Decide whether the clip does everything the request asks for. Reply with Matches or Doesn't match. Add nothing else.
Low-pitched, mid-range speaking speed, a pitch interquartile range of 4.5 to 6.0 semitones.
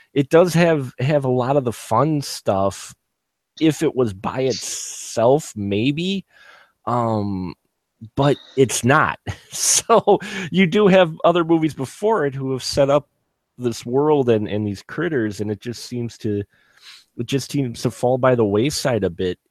Matches